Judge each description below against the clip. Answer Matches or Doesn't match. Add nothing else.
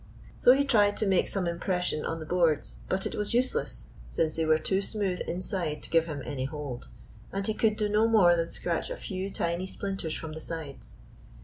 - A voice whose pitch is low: Doesn't match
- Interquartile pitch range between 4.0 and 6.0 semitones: Matches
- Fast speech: Matches